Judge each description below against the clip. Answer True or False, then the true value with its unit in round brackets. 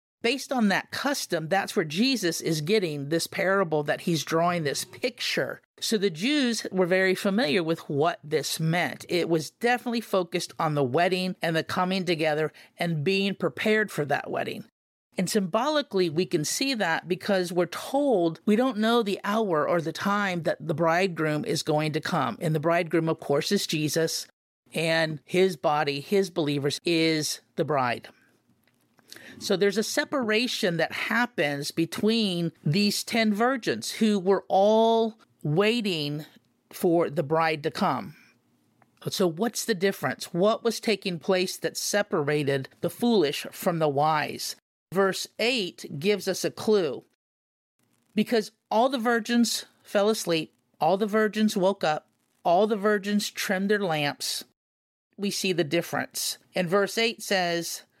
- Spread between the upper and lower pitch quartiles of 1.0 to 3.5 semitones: False (4.8 semitones)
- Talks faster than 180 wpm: False (150 wpm)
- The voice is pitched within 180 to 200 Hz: True (185 Hz)